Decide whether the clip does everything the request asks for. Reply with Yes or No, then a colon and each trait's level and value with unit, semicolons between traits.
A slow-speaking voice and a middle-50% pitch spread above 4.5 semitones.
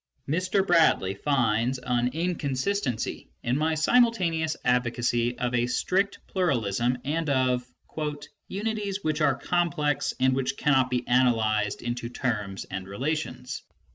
Yes: slow, 125 wpm; average, 5.1 semitones